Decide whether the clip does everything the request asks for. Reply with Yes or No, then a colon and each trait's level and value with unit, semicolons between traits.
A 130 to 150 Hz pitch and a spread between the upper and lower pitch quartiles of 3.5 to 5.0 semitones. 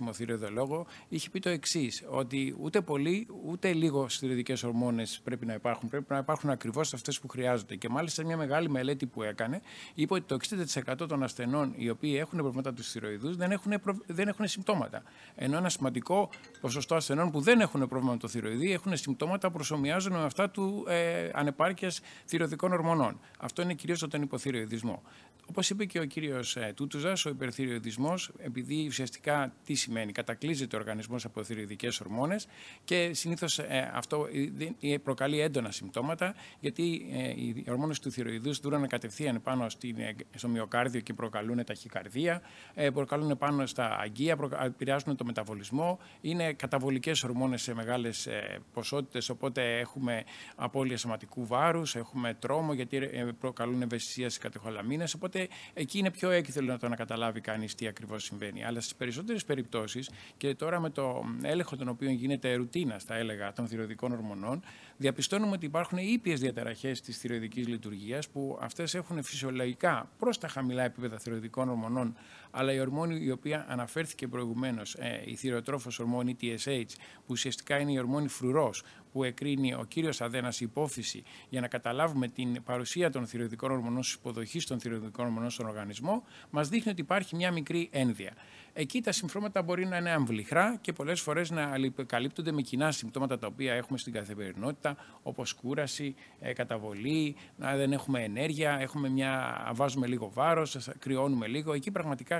Yes: low, 135 Hz; average, 4.7 semitones